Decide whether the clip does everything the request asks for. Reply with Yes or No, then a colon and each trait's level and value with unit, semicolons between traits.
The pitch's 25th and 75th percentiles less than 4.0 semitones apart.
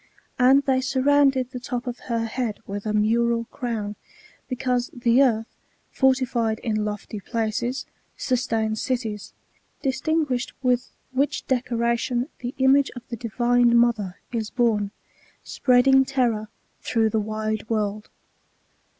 Yes: average, 2.8 semitones